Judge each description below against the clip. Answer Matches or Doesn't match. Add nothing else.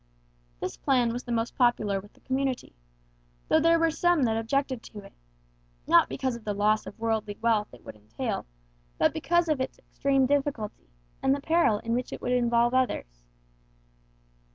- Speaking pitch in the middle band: Doesn't match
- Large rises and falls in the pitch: Doesn't match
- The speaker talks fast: Doesn't match